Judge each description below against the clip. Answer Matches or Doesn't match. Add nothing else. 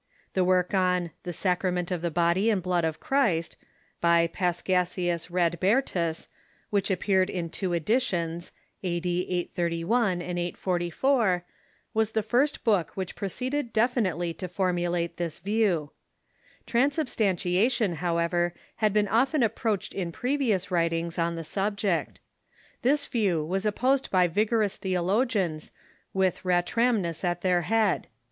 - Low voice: Doesn't match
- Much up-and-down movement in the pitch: Doesn't match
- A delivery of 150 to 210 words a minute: Doesn't match